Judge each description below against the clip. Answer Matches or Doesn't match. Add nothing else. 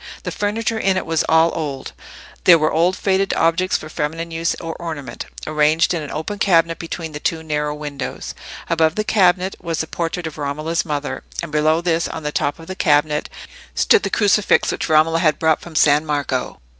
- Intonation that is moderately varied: Doesn't match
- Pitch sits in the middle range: Matches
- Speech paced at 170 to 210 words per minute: Matches